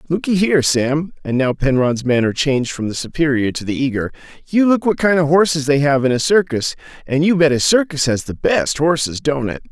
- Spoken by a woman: No, male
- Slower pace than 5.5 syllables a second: No, 5.6 syllables/s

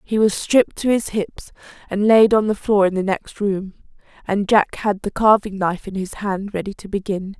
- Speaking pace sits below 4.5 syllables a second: No, 5.0 syllables/s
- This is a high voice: Yes, high, 205 Hz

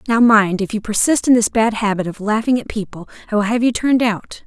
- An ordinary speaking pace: No, fast, 255 wpm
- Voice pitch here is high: Yes, high, 220 Hz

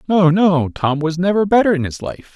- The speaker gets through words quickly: Yes, fast, 230 wpm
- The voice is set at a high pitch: No, medium, 175 Hz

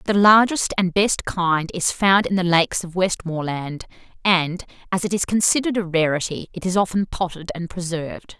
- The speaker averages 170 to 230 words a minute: Yes, average, 180 wpm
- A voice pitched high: No, medium, 180 Hz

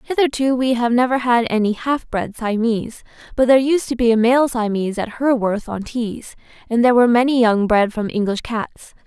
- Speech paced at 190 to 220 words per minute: Yes, average, 200 wpm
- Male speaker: No, female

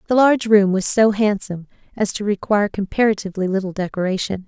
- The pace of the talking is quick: No, average, 160 wpm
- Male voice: No, female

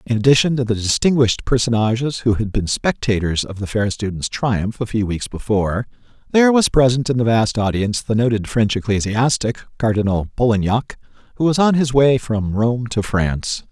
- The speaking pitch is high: No, low, 115 Hz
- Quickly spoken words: No, average, 180 wpm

